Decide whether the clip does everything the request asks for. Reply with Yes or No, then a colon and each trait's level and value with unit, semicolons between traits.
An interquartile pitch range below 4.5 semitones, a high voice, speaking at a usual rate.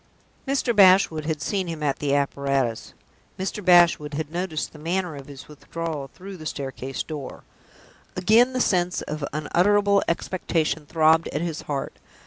No: average, 4.0 semitones; medium, 160 Hz; average, 155 wpm